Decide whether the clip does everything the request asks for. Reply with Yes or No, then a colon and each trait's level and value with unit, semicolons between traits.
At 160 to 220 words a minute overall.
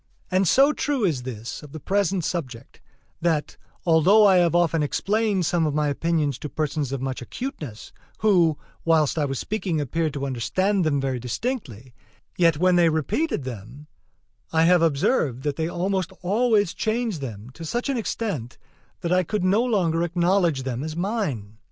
Yes: average, 170 wpm